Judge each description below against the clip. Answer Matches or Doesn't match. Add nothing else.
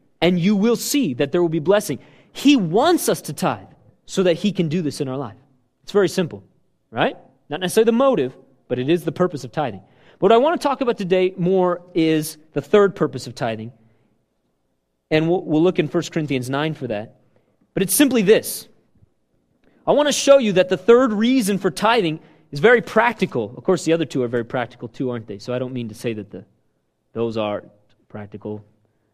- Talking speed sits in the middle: Doesn't match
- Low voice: Doesn't match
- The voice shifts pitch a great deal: Matches